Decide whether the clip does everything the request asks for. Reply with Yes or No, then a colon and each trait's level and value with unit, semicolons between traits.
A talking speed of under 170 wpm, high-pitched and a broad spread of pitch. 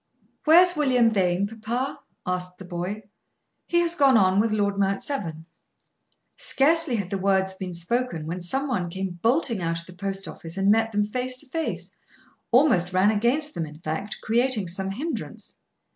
No: average, 175 wpm; high, 205 Hz; wide, 5.7 semitones